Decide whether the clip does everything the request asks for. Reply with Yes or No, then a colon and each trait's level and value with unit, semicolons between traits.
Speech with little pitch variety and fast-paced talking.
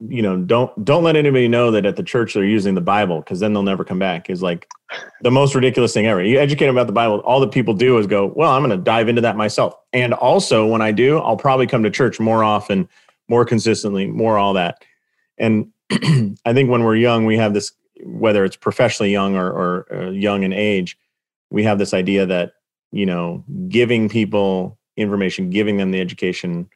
No: average, 3.4 semitones; fast, 220 wpm